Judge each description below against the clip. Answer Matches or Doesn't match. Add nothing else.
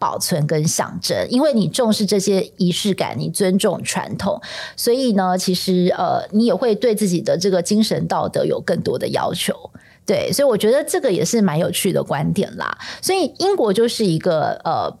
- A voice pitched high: Matches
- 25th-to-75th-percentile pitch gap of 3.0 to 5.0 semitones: Matches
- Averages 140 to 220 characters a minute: Doesn't match